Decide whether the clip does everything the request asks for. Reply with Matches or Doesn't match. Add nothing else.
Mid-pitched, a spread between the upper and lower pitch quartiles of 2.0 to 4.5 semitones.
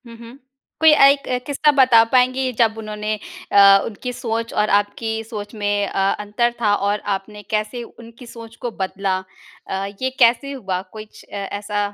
Doesn't match